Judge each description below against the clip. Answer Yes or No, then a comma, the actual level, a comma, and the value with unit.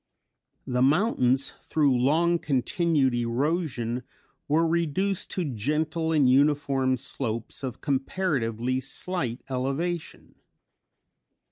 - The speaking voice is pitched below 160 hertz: Yes, medium, 140 Hz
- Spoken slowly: Yes, slow, 90 wpm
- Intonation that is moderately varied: Yes, average, 4.4 semitones